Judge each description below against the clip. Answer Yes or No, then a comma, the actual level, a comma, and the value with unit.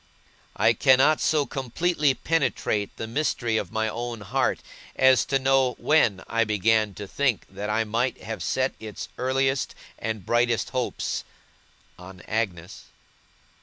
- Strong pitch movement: No, average, 3.6 semitones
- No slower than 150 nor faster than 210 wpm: No, slow, 135 wpm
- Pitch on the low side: Yes, low, 115 Hz